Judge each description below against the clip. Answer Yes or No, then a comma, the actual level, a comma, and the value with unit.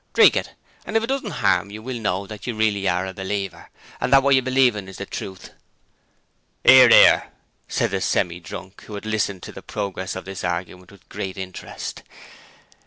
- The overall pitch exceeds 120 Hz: No, low, 100 Hz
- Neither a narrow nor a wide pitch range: Yes, average, 4.1 semitones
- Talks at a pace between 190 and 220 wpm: Yes, average, 195 wpm